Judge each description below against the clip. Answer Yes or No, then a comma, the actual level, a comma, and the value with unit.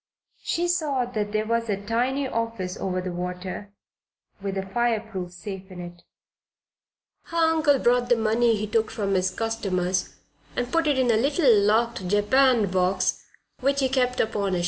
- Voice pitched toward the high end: Yes, high, 220 Hz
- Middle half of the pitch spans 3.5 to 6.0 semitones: Yes, average, 4.6 semitones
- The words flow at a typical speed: Yes, average, 170 wpm